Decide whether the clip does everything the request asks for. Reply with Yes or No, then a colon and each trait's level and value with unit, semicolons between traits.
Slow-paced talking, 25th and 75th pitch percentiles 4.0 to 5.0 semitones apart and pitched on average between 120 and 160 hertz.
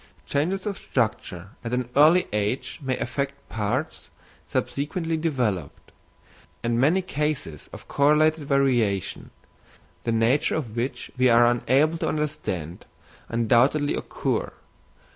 Yes: slow, 115 wpm; average, 4.6 semitones; low, 135 Hz